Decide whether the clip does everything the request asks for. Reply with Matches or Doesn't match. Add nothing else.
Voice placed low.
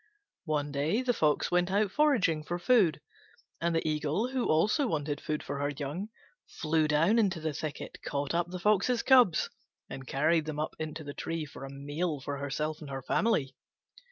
Doesn't match